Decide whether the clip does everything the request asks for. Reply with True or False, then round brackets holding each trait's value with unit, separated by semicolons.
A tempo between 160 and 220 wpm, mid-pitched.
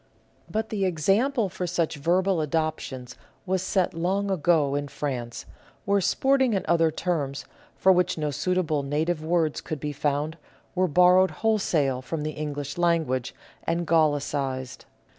False (140 wpm; 165 Hz)